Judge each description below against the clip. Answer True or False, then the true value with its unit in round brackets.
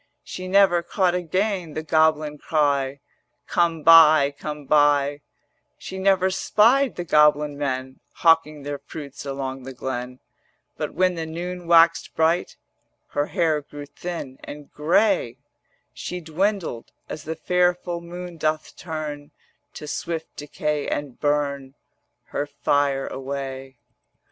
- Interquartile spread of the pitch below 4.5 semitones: True (3.4 semitones)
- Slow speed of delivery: True (130 wpm)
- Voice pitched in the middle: True (155 Hz)